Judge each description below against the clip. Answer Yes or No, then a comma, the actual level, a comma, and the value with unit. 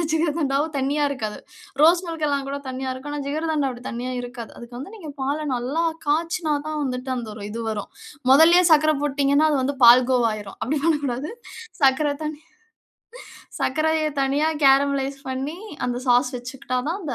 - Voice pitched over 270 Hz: Yes, very high, 280 Hz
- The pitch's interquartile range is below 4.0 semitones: Yes, average, 3.3 semitones